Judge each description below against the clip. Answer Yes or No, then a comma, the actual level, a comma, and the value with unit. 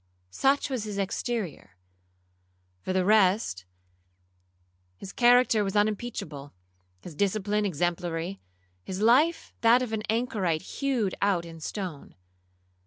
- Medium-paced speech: No, slow, 105 wpm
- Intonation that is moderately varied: No, wide, 6.0 semitones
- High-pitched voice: Yes, high, 195 Hz